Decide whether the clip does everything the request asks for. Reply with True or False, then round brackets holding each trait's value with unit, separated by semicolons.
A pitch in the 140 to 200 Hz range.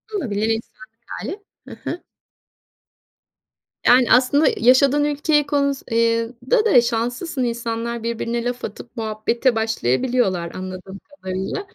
False (235 Hz)